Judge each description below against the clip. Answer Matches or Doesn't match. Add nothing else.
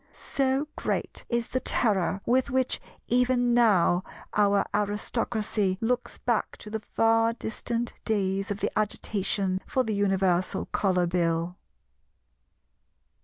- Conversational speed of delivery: Doesn't match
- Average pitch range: Matches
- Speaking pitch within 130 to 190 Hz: Doesn't match